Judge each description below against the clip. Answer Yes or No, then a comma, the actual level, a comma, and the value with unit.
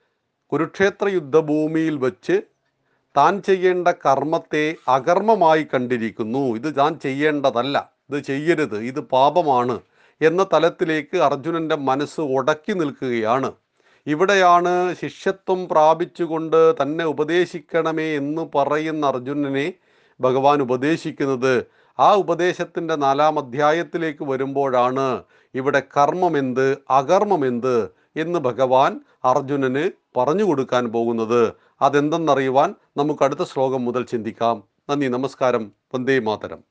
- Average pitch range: Yes, average, 3.7 semitones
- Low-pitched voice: No, medium, 145 Hz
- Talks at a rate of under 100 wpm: Yes, average, 90 wpm